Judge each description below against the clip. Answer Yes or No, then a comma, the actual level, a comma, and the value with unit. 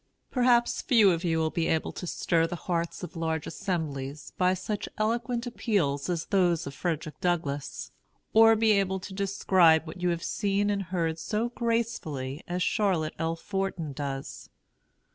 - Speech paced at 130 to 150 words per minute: No, average, 160 wpm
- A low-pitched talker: No, medium, 180 Hz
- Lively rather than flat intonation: No, average, 4.1 semitones